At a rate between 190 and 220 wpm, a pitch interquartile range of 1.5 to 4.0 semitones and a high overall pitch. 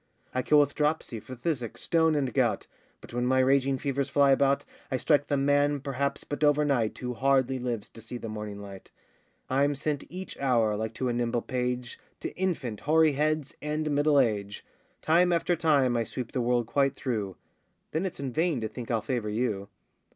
No: average, 195 wpm; average, 3.5 semitones; low, 135 Hz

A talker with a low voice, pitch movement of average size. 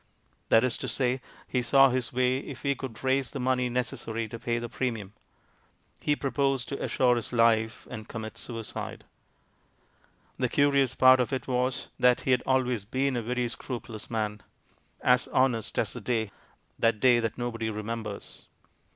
No: low, 125 Hz; narrow, 2.3 semitones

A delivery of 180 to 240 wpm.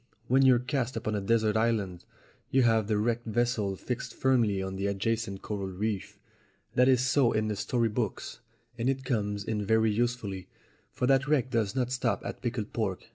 Yes: average, 185 wpm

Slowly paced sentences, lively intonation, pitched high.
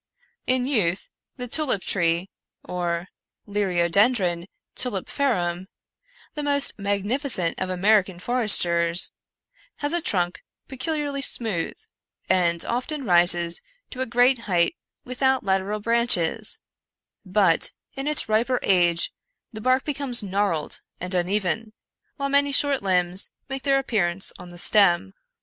Yes: slow, 120 wpm; wide, 6.4 semitones; high, 205 Hz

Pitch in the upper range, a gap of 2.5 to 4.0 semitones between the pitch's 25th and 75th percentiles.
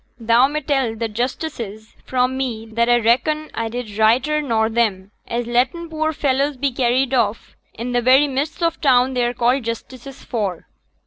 Yes: high, 245 Hz; average, 3.0 semitones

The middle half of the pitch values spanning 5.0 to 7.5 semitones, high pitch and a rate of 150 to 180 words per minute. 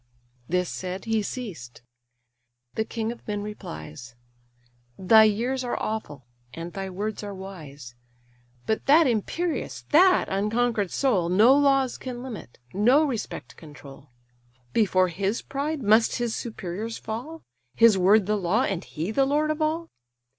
No: wide, 5.5 semitones; high, 215 Hz; average, 140 wpm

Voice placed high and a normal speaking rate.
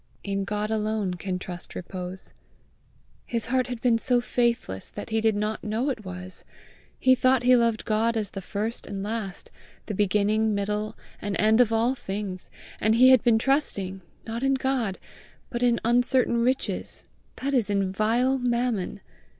Yes: high, 220 Hz; average, 165 wpm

